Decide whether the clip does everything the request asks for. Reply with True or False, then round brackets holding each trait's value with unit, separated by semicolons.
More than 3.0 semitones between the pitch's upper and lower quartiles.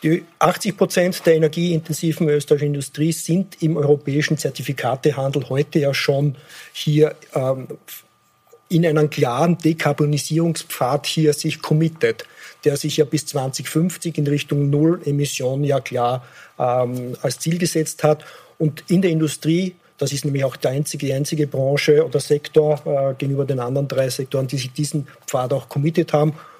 False (2.4 semitones)